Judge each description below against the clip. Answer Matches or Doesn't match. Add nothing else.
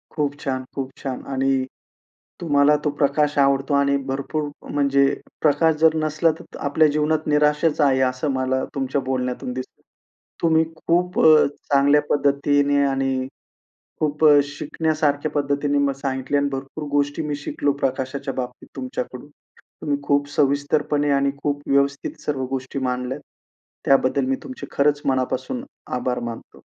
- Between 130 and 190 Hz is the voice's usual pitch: Matches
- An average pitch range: Doesn't match